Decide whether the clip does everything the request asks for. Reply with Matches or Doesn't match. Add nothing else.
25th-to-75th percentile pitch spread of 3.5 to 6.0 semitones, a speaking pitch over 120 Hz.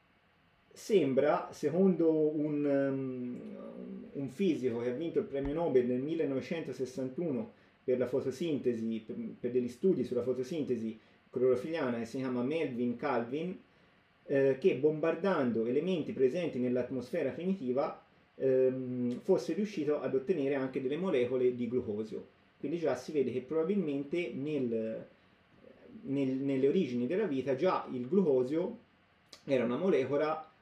Matches